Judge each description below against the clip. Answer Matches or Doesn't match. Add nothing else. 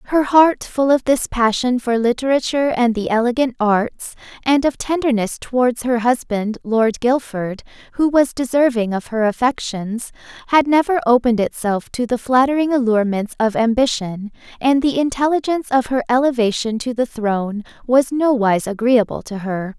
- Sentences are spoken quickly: Doesn't match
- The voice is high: Matches